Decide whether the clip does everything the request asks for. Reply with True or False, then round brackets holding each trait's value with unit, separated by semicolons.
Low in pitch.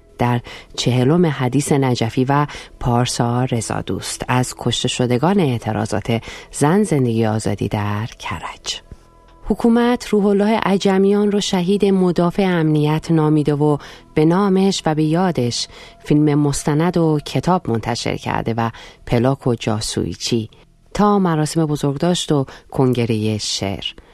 False (145 Hz)